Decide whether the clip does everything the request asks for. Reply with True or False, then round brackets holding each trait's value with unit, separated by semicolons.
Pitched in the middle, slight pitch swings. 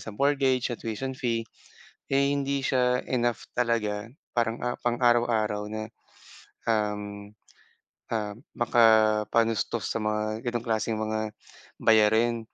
False (115 Hz; 2.1 semitones)